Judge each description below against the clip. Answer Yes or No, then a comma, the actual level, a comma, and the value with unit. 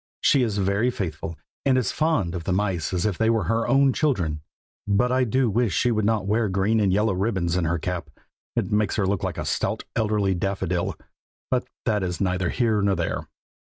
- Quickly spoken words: Yes, fast, 215 wpm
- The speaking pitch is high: No, low, 100 Hz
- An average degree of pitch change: Yes, average, 3.7 semitones